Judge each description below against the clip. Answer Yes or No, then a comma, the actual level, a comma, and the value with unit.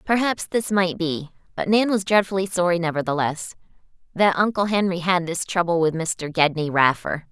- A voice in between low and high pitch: Yes, medium, 180 Hz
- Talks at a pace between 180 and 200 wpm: No, average, 165 wpm